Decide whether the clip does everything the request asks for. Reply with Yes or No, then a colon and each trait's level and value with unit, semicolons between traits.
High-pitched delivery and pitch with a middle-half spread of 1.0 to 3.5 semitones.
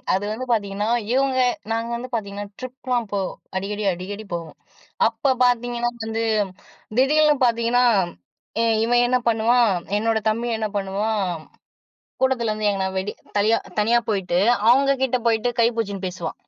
Yes: high, 225 Hz; average, 3.1 semitones